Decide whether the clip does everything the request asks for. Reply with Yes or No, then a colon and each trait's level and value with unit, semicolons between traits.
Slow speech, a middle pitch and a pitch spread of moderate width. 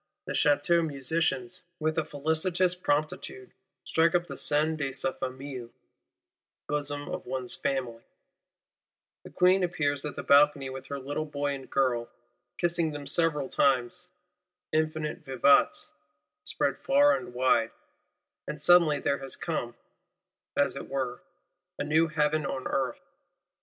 Yes: slow, 130 wpm; medium, 145 Hz; average, 3.4 semitones